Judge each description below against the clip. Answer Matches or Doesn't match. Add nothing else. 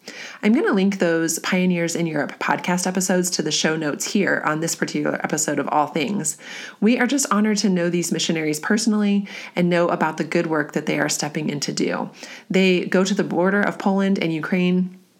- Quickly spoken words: Matches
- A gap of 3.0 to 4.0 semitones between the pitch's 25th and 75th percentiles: Matches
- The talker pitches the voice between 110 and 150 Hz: Doesn't match